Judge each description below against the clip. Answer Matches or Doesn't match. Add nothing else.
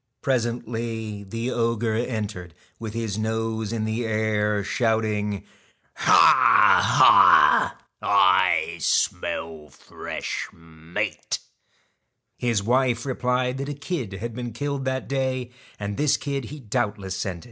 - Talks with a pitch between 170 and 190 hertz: Doesn't match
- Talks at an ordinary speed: Doesn't match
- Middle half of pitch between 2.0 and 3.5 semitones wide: Matches